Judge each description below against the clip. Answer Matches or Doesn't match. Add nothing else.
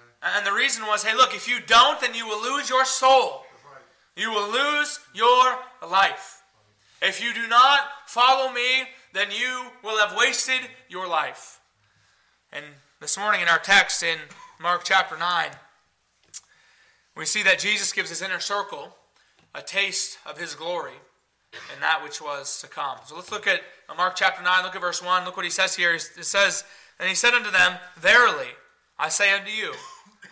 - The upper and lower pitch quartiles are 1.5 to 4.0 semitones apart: Doesn't match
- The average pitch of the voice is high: Matches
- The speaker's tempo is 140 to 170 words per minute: Doesn't match